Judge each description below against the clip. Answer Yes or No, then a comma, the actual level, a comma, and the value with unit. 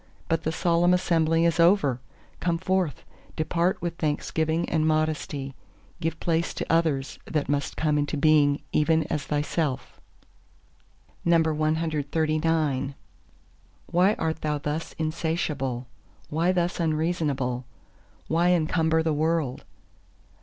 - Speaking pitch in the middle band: Yes, medium, 160 Hz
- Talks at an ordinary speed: No, slow, 110 wpm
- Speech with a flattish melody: Yes, narrow, 2.0 semitones